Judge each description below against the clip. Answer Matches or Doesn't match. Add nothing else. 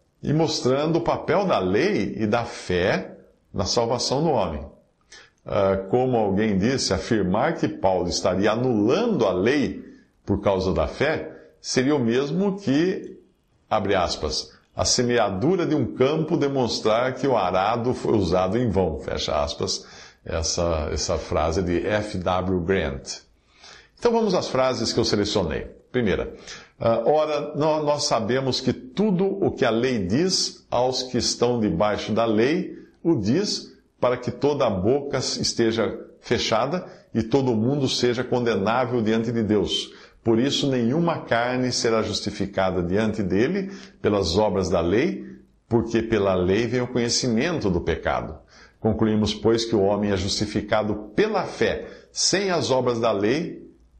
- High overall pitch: Doesn't match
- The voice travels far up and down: Doesn't match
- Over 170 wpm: Doesn't match